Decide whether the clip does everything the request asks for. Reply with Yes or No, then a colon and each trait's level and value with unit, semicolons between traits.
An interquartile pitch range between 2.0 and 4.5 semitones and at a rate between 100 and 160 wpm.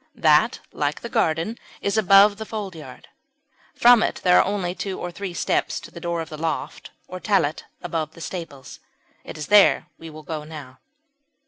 No: average, 4.0 semitones; average, 190 wpm